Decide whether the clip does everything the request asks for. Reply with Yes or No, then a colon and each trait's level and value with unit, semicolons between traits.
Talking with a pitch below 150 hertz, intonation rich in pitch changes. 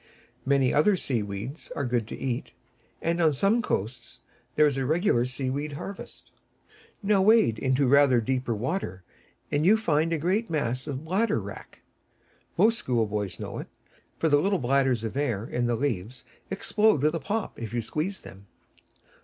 Yes: medium, 140 Hz; wide, 5.8 semitones